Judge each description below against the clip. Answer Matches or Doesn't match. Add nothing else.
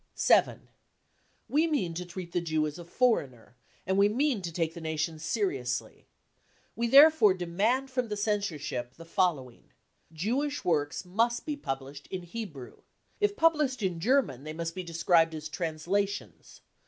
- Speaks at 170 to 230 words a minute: Doesn't match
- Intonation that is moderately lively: Doesn't match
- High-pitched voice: Doesn't match